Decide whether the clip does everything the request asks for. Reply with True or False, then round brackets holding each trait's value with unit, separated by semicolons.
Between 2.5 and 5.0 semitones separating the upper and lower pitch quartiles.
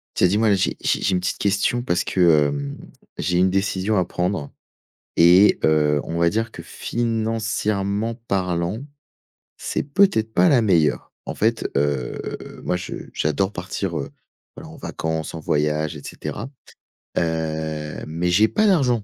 False (5.5 semitones)